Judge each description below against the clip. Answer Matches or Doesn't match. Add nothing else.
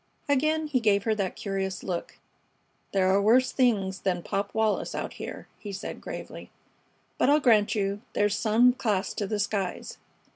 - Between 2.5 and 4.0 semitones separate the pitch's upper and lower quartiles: Matches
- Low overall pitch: Doesn't match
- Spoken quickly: Doesn't match